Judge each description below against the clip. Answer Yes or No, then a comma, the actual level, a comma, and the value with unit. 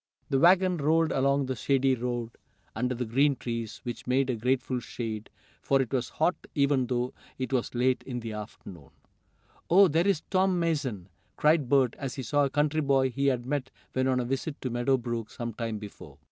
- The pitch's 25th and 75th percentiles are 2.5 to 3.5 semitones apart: Yes, average, 2.9 semitones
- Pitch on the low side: Yes, low, 130 Hz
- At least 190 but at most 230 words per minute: Yes, average, 200 wpm